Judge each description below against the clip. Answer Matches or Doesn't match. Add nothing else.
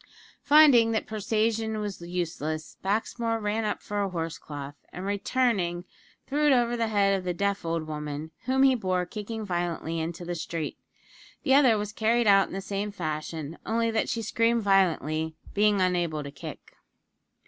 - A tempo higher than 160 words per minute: Matches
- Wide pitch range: Doesn't match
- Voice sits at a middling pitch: Doesn't match